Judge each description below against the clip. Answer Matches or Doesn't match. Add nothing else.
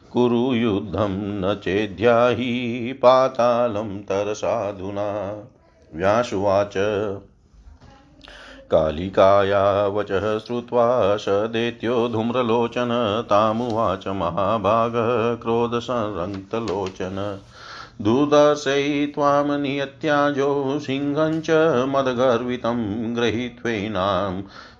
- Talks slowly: Matches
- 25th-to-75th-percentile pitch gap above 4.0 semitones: Doesn't match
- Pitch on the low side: Matches